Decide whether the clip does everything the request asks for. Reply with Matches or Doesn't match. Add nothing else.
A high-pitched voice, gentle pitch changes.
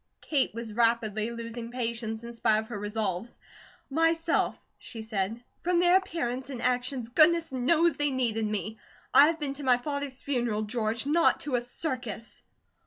Doesn't match